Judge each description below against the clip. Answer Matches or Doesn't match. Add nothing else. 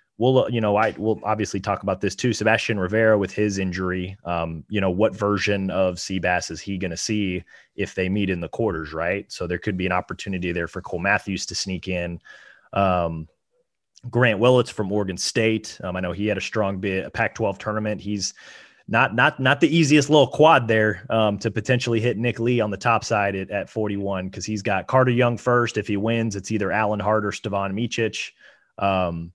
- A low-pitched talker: Matches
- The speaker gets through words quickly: Matches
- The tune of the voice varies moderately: Matches